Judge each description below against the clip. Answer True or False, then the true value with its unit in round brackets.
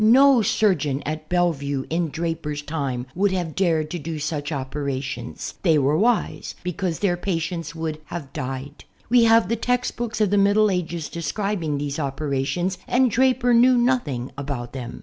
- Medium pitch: True (165 Hz)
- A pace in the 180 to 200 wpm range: False (165 wpm)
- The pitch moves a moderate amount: False (6.1 semitones)